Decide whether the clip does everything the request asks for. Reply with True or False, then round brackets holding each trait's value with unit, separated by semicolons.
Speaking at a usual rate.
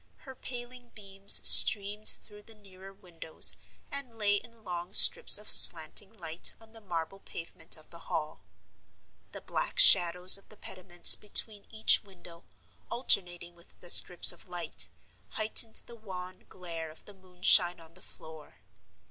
True (150 wpm)